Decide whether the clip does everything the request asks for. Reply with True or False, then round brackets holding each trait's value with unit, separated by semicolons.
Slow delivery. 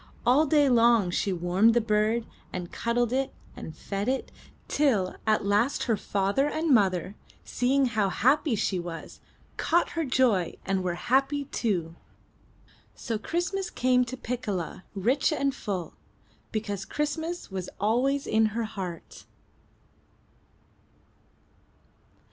True (130 wpm)